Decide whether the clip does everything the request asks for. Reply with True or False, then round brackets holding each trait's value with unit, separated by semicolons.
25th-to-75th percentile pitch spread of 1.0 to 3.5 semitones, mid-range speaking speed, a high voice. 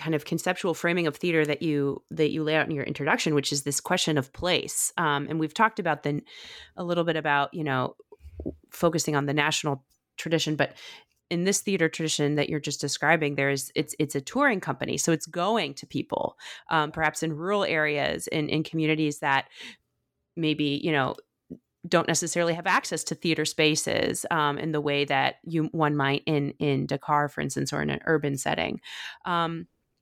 False (2.5 semitones; 195 wpm; 155 Hz)